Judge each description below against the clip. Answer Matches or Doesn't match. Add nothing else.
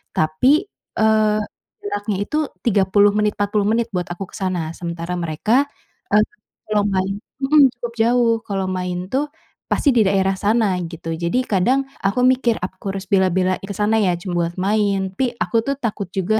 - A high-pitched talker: Matches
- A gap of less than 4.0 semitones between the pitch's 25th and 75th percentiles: Matches